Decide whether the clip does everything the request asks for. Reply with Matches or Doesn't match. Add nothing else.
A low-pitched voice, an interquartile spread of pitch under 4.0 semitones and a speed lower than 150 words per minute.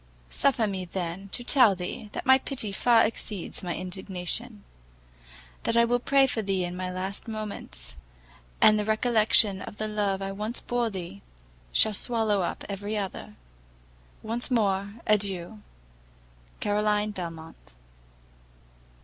Doesn't match